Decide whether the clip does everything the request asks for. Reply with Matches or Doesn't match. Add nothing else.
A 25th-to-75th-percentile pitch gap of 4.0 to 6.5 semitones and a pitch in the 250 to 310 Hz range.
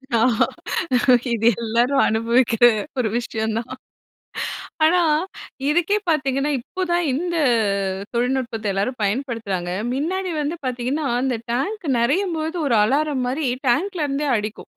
Matches